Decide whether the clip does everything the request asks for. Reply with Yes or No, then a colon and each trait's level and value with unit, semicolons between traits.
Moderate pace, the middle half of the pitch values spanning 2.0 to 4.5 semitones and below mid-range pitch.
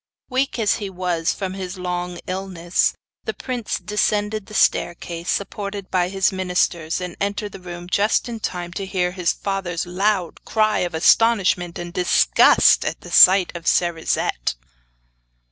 No: average, 150 wpm; narrow, 2.4 semitones; medium, 185 Hz